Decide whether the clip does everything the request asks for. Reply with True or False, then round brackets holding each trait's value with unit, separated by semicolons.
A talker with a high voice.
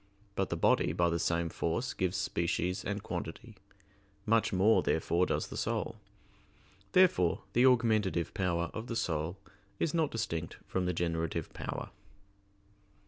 False (90 Hz)